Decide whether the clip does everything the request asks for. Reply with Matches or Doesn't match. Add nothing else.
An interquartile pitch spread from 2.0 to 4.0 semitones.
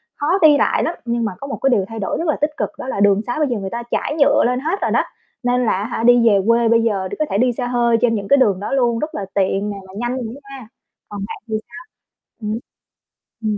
Matches